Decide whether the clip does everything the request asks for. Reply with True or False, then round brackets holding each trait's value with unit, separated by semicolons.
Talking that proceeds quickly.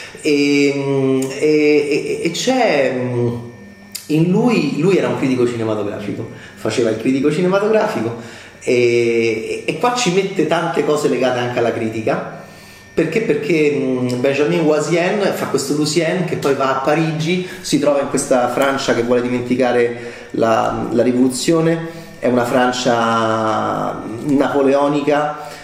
False (125 wpm)